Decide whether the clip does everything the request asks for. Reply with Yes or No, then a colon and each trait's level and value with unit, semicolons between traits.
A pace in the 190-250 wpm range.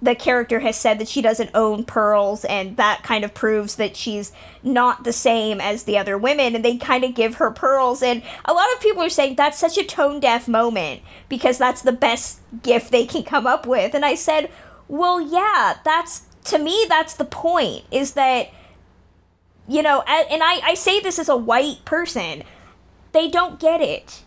Yes: fast, 205 wpm